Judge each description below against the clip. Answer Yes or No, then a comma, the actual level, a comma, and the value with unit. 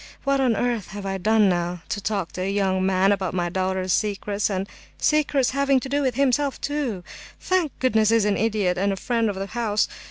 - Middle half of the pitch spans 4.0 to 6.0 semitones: Yes, average, 4.9 semitones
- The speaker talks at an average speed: No, fast, 210 wpm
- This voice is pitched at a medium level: No, high, 210 Hz